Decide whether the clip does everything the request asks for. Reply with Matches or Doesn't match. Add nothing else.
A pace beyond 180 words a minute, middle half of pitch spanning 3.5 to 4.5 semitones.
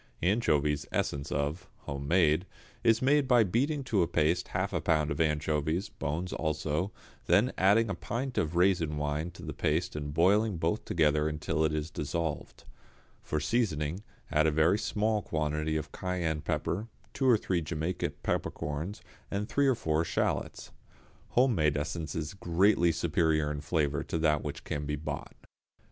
Doesn't match